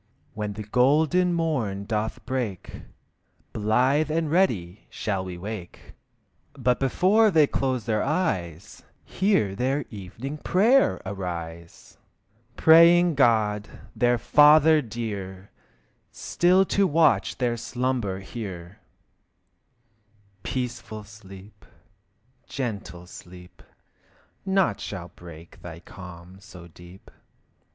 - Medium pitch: No, low, 110 Hz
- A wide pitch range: Yes, wide, 7.7 semitones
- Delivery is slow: Yes, slow, 95 wpm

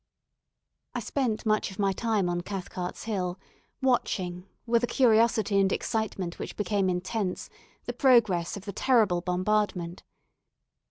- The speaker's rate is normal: No, slow, 130 wpm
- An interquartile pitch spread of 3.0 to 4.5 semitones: Yes, average, 3.7 semitones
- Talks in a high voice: Yes, high, 200 Hz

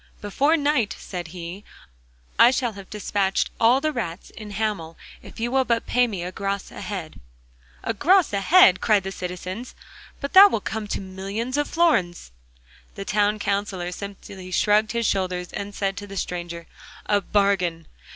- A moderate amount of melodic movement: Yes, average, 3.8 semitones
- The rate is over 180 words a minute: No, average, 170 wpm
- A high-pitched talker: Yes, high, 200 Hz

